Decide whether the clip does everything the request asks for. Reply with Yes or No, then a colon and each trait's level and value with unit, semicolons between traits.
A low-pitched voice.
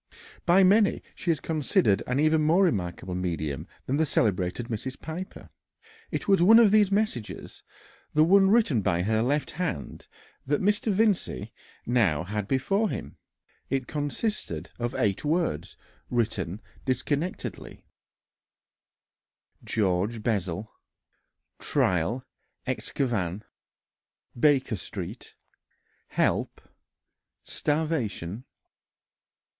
Yes: low, 130 Hz